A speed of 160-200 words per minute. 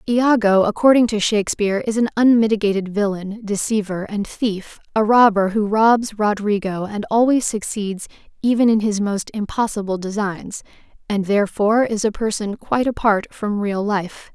No: average, 145 wpm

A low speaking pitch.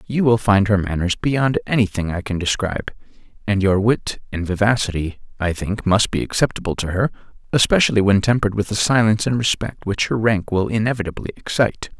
Yes: low, 105 Hz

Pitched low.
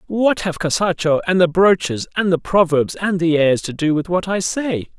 No: medium, 175 Hz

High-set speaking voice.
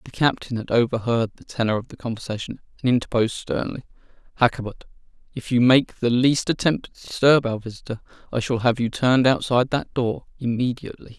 No: low, 120 Hz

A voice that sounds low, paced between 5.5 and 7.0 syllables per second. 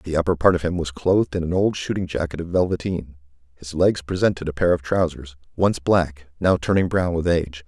Yes: very low, 85 Hz; 5.6 syllables/s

